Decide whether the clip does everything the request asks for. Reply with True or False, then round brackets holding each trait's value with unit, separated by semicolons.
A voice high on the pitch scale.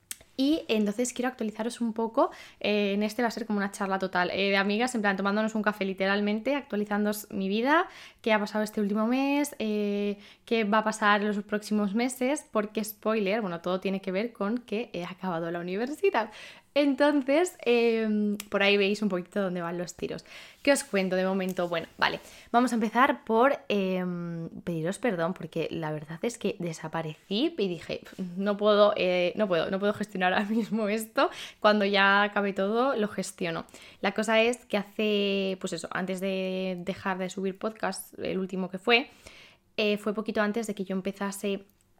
True (205 Hz)